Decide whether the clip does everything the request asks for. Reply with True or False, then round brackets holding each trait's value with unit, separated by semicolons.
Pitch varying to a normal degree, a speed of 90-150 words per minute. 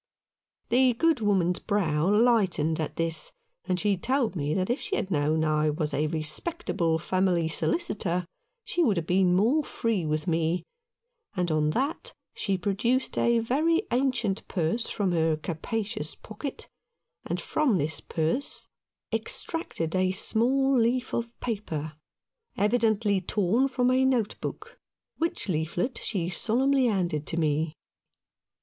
False (6.8 semitones; 140 wpm)